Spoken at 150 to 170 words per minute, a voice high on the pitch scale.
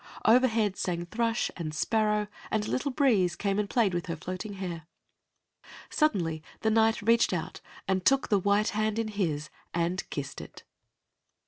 Yes: average, 160 wpm; high, 205 Hz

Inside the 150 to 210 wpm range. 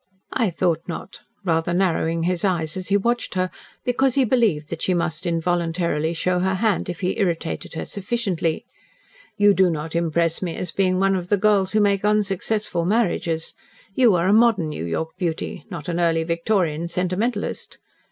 Yes: average, 175 wpm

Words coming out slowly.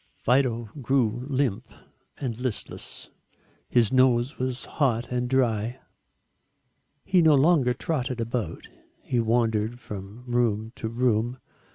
Yes: slow, 110 wpm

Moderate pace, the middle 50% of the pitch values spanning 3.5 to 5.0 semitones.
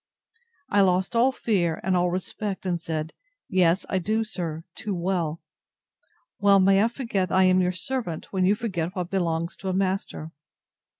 No: average, 170 wpm; narrow, 2.6 semitones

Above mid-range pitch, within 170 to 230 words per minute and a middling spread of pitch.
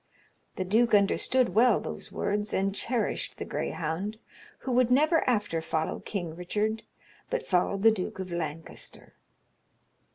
No: high, 205 Hz; slow, 135 wpm; average, 4.6 semitones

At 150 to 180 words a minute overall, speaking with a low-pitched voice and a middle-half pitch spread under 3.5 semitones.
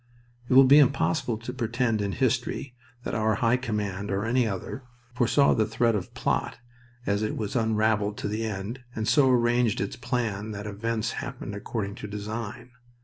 Yes: average, 175 wpm; low, 110 Hz; average, 2.8 semitones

